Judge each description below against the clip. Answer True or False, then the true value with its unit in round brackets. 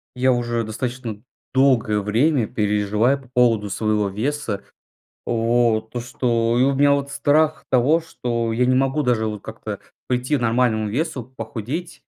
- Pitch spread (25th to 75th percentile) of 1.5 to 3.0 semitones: False (3.4 semitones)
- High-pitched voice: False (120 Hz)